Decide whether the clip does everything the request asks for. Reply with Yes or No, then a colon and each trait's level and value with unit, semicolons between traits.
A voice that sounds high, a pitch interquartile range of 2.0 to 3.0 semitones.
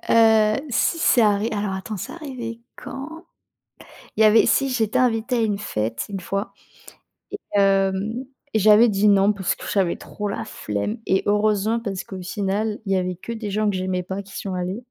Yes: high, 210 Hz; average, 2.7 semitones